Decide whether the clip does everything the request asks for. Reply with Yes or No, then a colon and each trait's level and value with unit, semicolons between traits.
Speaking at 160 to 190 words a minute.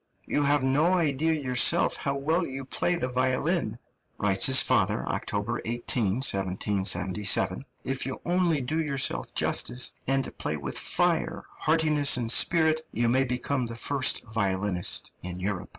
No: average, 145 wpm